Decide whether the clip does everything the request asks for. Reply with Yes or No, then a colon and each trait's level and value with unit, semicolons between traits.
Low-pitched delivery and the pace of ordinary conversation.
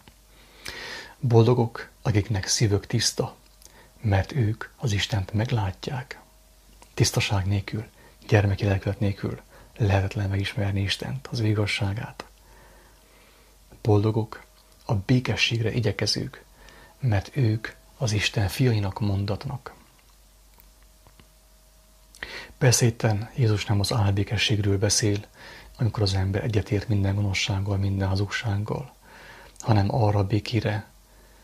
No: low, 105 Hz; slow, 90 wpm